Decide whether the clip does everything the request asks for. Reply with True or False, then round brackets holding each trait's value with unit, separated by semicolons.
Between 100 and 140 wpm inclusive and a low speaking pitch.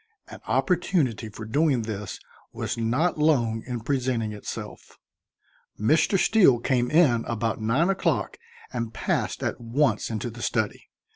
True (135 wpm; 120 Hz)